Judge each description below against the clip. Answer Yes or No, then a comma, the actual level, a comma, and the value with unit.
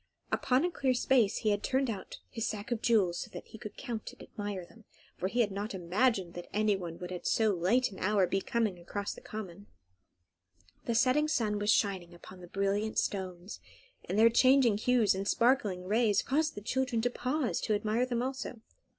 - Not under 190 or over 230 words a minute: Yes, average, 200 wpm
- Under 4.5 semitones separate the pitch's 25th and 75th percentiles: Yes, average, 4.0 semitones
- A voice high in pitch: Yes, high, 215 Hz